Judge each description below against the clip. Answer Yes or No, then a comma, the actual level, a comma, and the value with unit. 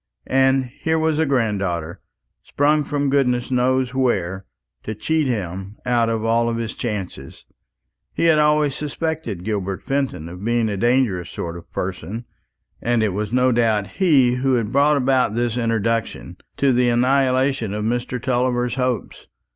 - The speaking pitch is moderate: No, low, 120 Hz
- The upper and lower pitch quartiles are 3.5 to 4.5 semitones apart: Yes, average, 3.9 semitones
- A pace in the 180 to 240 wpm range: No, average, 155 wpm